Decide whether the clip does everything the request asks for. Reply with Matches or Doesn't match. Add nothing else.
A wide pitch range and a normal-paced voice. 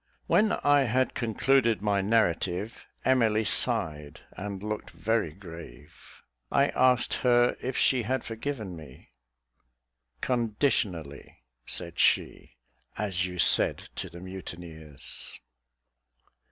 Doesn't match